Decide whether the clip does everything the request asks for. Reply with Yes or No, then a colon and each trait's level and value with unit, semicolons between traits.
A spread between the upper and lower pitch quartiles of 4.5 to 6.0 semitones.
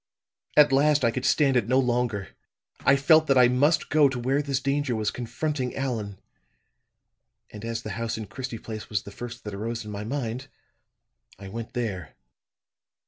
No: average, 3.8 semitones